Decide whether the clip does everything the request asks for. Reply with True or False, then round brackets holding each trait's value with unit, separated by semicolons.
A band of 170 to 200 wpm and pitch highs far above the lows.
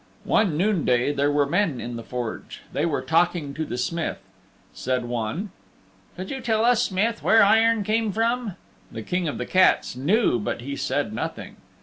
True (180 wpm; 8.7 semitones)